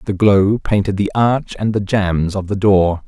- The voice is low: Yes, low, 100 Hz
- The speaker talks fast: Yes, fast, 215 wpm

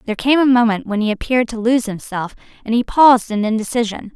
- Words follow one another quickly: Yes, fast, 215 wpm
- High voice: Yes, high, 230 Hz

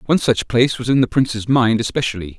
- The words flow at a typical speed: No, fast, 225 wpm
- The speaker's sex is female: No, male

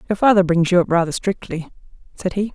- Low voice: No, medium, 185 Hz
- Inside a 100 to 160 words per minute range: No, fast, 210 wpm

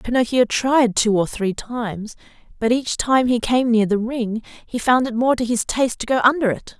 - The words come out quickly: Yes, fast, 220 wpm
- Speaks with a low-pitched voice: No, high, 235 Hz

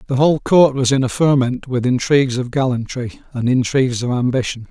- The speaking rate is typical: Yes, average, 190 wpm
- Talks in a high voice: No, low, 130 Hz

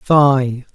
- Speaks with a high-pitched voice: No, low, 135 Hz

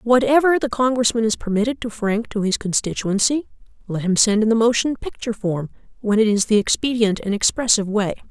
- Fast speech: No, average, 190 wpm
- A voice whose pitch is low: No, high, 225 Hz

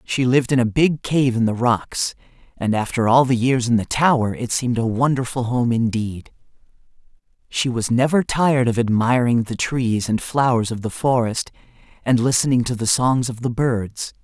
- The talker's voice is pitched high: No, low, 120 Hz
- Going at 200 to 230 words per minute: No, average, 185 wpm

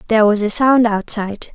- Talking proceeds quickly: No, average, 195 wpm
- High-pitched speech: Yes, high, 215 Hz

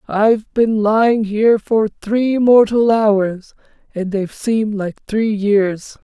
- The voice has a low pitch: No, high, 215 Hz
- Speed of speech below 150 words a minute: Yes, slow, 135 wpm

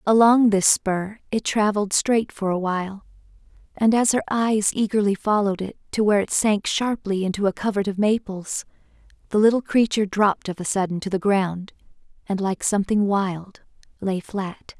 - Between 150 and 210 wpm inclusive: Yes, average, 170 wpm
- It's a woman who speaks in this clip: Yes, female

